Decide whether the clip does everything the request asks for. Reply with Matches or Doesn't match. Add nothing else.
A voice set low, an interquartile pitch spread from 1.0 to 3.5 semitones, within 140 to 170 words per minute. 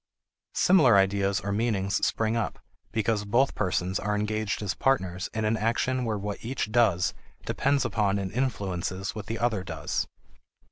Matches